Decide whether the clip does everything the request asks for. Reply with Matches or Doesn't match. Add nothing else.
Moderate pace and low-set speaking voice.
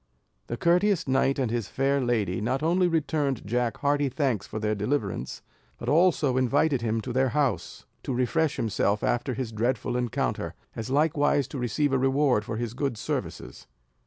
Matches